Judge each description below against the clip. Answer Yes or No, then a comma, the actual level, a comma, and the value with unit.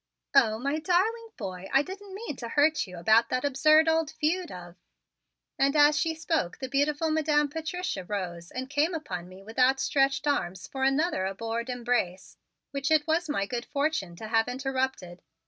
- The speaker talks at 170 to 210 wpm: Yes, average, 180 wpm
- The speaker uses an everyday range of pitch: No, wide, 6.2 semitones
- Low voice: No, very high, 270 Hz